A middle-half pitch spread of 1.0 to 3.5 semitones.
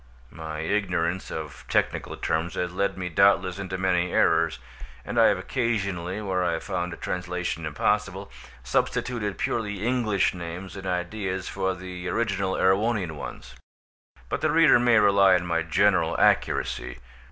Yes: narrow, 2.4 semitones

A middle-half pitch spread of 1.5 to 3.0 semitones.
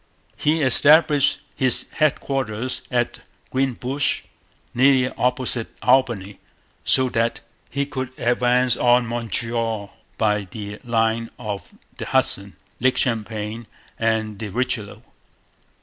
Yes: average, 2.7 semitones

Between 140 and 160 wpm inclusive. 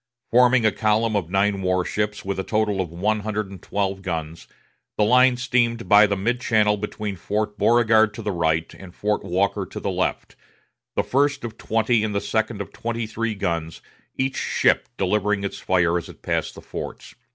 No: average, 195 wpm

